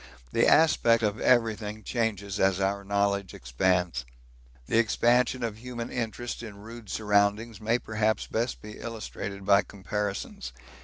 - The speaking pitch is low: Yes, low, 105 Hz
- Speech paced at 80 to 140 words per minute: Yes, slow, 135 wpm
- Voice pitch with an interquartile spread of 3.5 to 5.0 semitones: No, narrow, 2.6 semitones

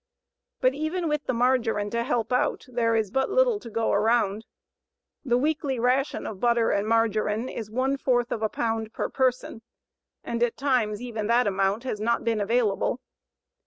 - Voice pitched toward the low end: No, high, 235 Hz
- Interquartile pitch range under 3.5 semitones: Yes, average, 2.7 semitones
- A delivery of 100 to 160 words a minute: No, average, 175 wpm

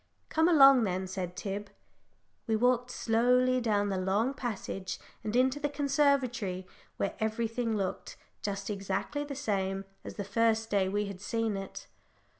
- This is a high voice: Yes, high, 220 Hz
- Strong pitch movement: No, average, 4.2 semitones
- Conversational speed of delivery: Yes, average, 150 wpm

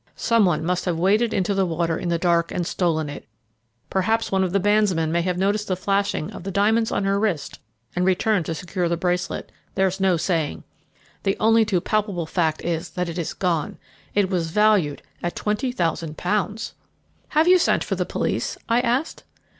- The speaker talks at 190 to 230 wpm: Yes, average, 195 wpm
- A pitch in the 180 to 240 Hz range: Yes, medium, 185 Hz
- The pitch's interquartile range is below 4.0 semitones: Yes, average, 3.5 semitones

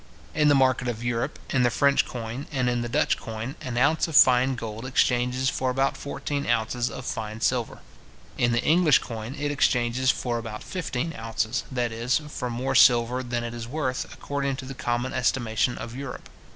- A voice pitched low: Yes, low, 125 Hz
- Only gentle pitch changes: Yes, narrow, 2.2 semitones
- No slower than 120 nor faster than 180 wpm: No, average, 190 wpm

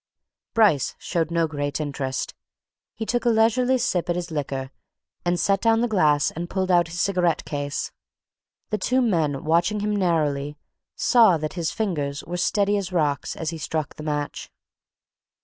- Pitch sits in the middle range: Yes, medium, 170 Hz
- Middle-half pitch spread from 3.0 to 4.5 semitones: No, wide, 5.5 semitones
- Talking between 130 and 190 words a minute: Yes, average, 165 wpm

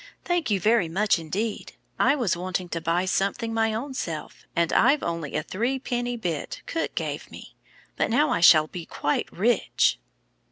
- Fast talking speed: No, average, 165 wpm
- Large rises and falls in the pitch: Yes, wide, 6.1 semitones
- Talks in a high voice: Yes, high, 195 Hz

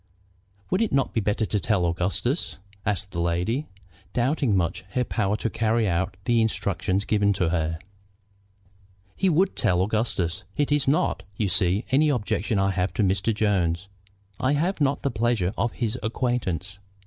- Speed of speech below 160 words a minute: No, average, 165 wpm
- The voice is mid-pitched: No, low, 105 Hz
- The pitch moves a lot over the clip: No, average, 4.8 semitones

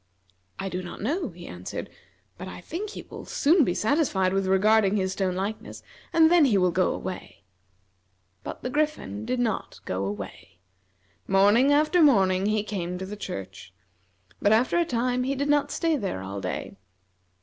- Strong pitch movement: Yes, wide, 7.0 semitones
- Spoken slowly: No, average, 175 wpm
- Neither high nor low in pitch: No, high, 205 Hz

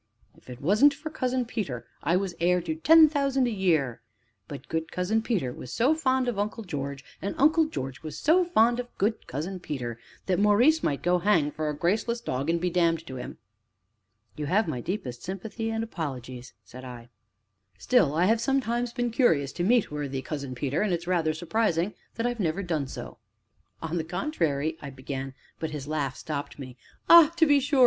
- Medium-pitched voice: Yes, medium, 175 Hz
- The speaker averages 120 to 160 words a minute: No, average, 200 wpm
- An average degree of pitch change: No, wide, 8.4 semitones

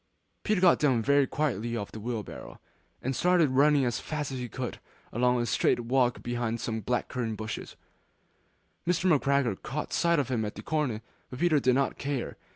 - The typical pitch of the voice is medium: No, low, 130 Hz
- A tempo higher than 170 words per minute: Yes, average, 190 wpm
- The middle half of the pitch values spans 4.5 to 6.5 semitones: No, average, 3.7 semitones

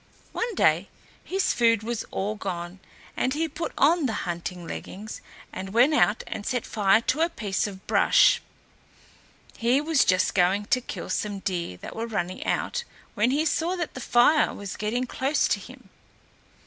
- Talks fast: No, average, 175 wpm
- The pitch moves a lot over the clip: Yes, wide, 6.5 semitones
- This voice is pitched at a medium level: No, high, 225 Hz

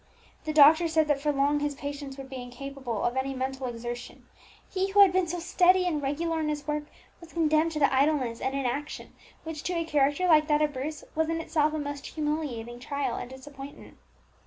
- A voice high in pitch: Yes, very high, 295 Hz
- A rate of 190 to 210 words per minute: Yes, fast, 205 wpm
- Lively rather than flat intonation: No, average, 2.8 semitones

